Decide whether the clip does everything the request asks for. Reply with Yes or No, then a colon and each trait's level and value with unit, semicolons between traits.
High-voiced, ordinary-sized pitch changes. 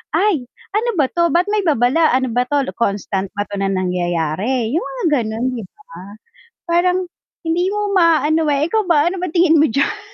No: very high, 290 Hz; wide, 6.9 semitones